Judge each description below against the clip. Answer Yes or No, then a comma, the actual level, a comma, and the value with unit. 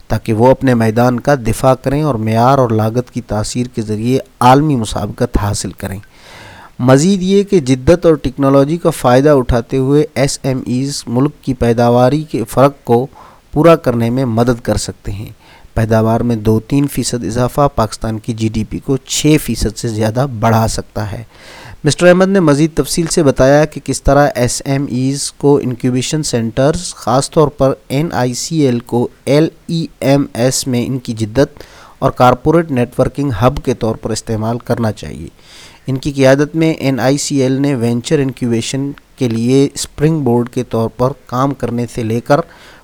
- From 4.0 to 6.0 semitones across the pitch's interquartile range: No, average, 3.3 semitones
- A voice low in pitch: Yes, low, 130 Hz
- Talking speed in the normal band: Yes, average, 180 wpm